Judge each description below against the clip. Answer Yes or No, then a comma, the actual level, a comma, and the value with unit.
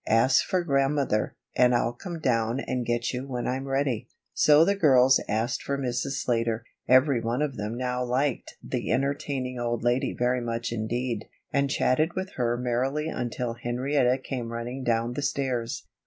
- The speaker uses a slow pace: No, average, 170 wpm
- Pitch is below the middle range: Yes, low, 125 Hz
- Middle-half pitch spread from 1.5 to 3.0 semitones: Yes, narrow, 2.6 semitones